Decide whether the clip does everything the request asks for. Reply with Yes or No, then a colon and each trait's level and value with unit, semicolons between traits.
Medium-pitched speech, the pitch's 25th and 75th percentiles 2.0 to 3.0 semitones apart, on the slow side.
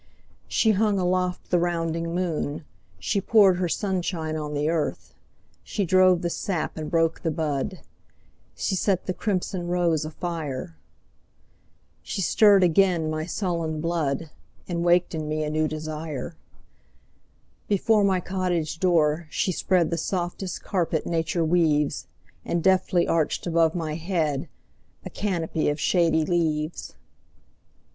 Yes: medium, 170 Hz; average, 2.7 semitones; slow, 115 wpm